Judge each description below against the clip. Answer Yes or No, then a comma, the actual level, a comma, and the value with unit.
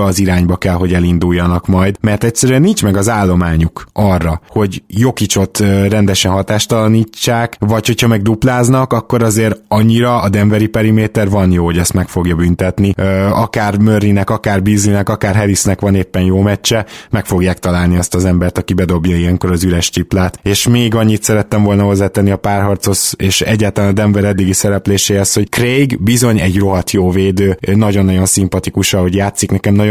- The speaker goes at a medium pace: No, fast, 165 wpm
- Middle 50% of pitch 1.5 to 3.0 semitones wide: Yes, average, 2.7 semitones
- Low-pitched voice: Yes, low, 100 Hz